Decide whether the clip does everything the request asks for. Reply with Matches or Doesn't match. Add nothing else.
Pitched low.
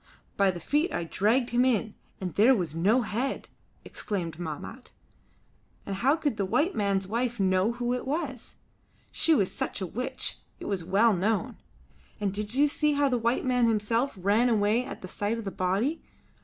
Doesn't match